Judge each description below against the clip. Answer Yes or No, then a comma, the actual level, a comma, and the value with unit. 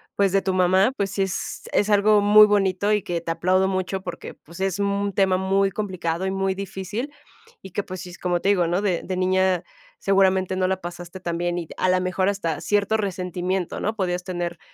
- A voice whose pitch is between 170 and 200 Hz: Yes, high, 190 Hz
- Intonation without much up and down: Yes, narrow, 1.8 semitones